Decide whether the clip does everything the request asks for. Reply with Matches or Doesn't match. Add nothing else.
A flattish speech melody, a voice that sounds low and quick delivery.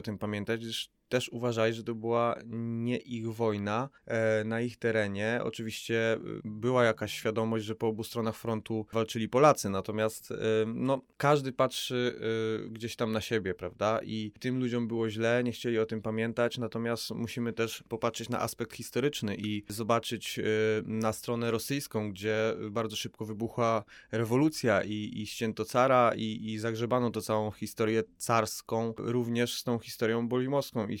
Matches